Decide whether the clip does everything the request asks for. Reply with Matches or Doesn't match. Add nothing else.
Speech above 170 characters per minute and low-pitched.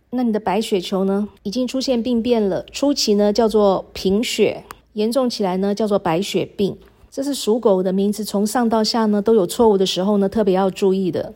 Doesn't match